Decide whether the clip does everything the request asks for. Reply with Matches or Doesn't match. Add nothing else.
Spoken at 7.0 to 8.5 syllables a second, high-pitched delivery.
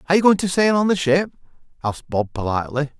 Doesn't match